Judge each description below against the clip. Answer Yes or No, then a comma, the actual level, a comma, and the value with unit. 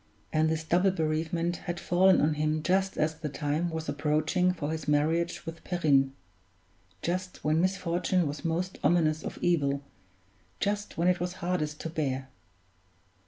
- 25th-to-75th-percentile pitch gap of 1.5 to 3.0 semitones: Yes, average, 2.7 semitones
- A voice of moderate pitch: Yes, medium, 160 Hz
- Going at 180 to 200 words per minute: No, average, 155 wpm